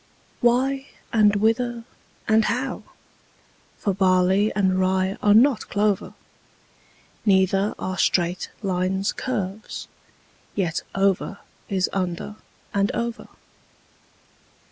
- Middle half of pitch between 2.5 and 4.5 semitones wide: Yes, average, 3.0 semitones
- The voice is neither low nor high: No, high, 200 Hz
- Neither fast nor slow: No, slow, 95 wpm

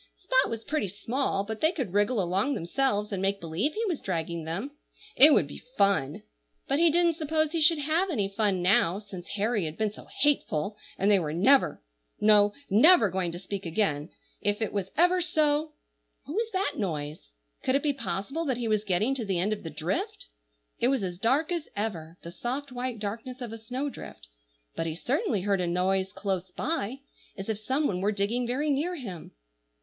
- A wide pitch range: Yes, wide, 6.9 semitones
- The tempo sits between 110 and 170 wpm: No, average, 195 wpm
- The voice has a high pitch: Yes, high, 210 Hz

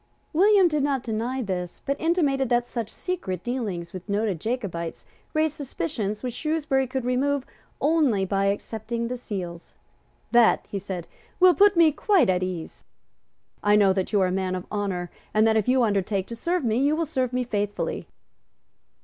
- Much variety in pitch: Yes, wide, 6.1 semitones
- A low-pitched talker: No, high, 230 Hz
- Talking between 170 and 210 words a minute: Yes, average, 175 wpm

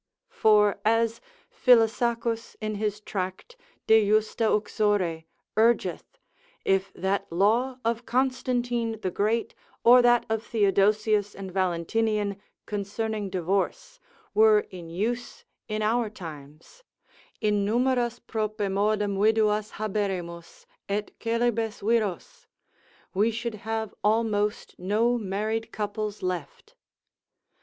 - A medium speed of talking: No, slow, 100 wpm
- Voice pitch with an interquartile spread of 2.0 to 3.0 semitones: Yes, narrow, 2.4 semitones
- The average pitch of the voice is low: No, high, 215 Hz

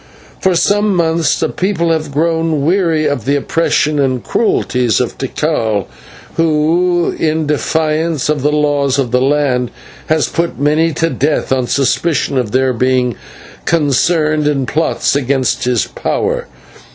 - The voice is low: No, medium, 150 Hz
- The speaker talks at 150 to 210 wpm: No, average, 140 wpm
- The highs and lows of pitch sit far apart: No, average, 3.7 semitones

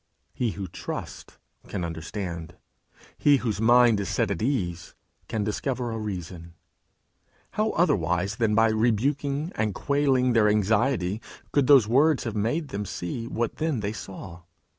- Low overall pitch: Yes, low, 110 Hz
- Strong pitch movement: No, average, 4.9 semitones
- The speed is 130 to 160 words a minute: Yes, average, 145 wpm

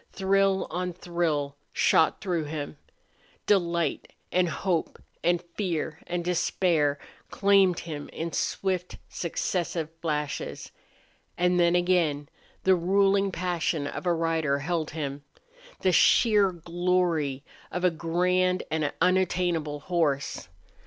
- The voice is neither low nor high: Yes, medium, 175 Hz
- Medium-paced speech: No, slow, 110 wpm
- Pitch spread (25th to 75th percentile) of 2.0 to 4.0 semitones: Yes, narrow, 2.6 semitones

